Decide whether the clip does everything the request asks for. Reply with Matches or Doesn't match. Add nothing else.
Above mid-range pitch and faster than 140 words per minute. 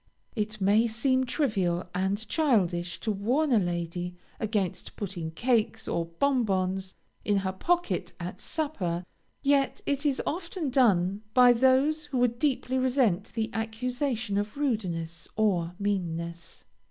Doesn't match